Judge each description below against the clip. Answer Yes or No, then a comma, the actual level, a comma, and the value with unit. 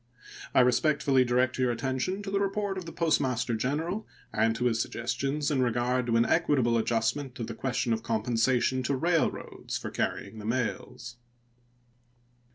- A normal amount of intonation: Yes, average, 3.9 semitones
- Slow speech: No, average, 160 wpm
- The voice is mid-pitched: No, low, 125 Hz